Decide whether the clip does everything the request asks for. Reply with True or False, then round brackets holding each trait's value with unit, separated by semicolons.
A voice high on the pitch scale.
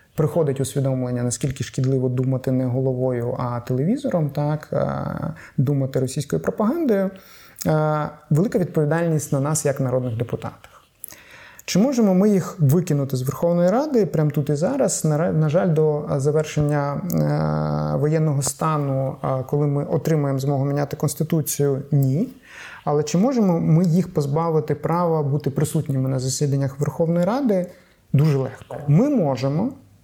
False (150 Hz)